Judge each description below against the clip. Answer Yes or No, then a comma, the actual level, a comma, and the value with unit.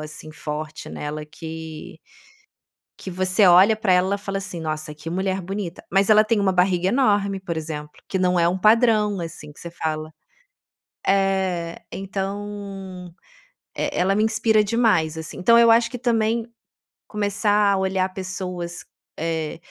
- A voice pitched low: No, high, 190 Hz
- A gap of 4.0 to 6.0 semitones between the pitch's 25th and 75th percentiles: No, average, 3.6 semitones